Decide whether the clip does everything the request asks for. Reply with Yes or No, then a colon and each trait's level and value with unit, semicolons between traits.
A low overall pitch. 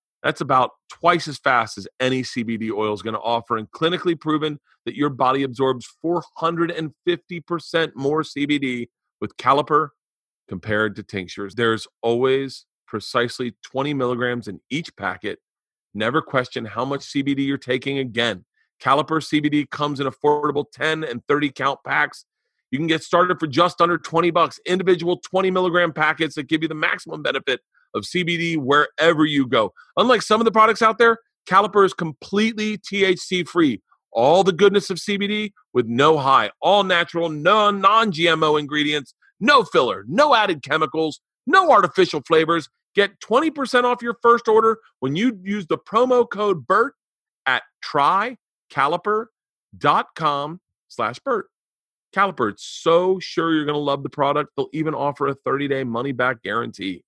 No: medium, 155 Hz